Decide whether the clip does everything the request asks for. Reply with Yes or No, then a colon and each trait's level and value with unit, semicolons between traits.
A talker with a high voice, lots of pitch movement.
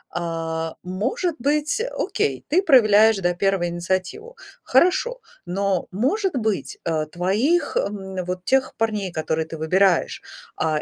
Yes: high, 195 Hz; wide, 7.4 semitones